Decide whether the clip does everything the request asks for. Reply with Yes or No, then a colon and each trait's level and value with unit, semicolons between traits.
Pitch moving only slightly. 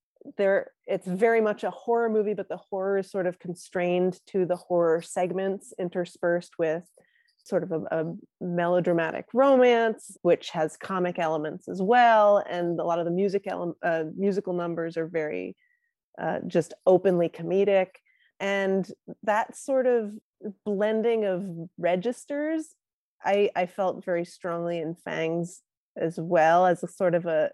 No: average, 3.5 semitones